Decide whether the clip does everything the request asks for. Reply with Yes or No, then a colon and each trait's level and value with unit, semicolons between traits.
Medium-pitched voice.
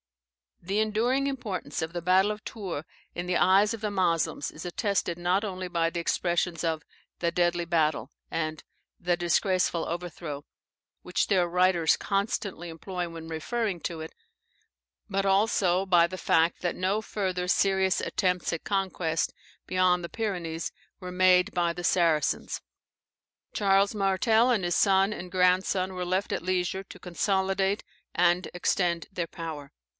Yes: medium, 180 Hz